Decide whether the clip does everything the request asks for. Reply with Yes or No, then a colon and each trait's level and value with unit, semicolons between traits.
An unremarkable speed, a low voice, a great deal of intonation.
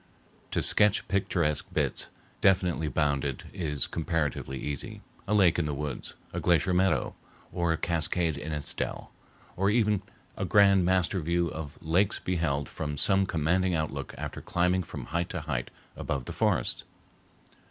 No: average, 150 wpm; very low, 85 Hz; average, 3.7 semitones